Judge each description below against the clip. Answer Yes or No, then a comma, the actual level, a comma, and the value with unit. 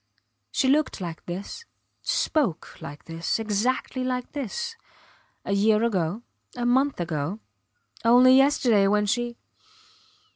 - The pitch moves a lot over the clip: No, average, 4.8 semitones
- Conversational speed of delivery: No, slow, 115 wpm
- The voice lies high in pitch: Yes, high, 225 Hz